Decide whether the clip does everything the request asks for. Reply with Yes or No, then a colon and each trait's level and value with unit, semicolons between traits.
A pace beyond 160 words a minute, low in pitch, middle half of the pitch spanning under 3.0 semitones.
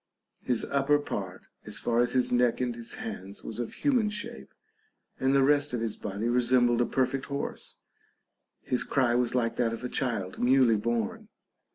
Yes: average, 180 wpm; low, 120 Hz; narrow, 2.5 semitones